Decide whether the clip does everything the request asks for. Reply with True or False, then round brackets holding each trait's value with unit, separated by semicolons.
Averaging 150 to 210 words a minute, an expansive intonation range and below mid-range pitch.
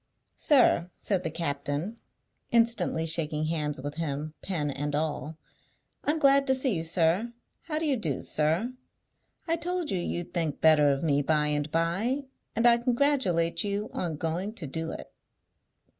False (160 wpm; 7.5 semitones; 165 Hz)